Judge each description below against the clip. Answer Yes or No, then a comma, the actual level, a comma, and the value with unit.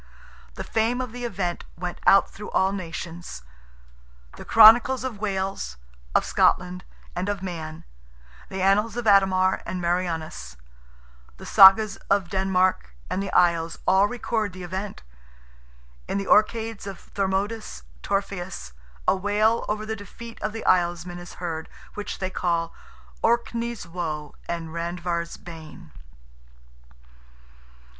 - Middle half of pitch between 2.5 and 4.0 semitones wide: Yes, average, 3.4 semitones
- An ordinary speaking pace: No, slow, 130 wpm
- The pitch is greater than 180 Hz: Yes, high, 190 Hz